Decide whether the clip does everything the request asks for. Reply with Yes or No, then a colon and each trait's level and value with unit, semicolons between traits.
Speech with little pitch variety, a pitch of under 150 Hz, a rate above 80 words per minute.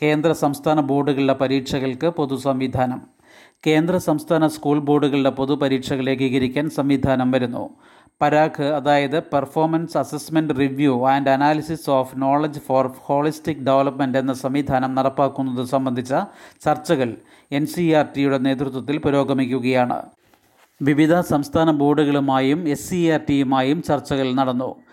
Yes: narrow, 2.1 semitones; medium, 140 Hz; average, 115 wpm